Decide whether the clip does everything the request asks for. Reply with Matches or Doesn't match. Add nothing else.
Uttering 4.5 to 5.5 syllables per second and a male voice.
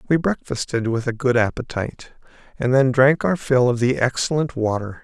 Matches